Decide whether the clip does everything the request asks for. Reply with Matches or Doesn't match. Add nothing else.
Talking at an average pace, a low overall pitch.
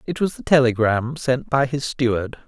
Matches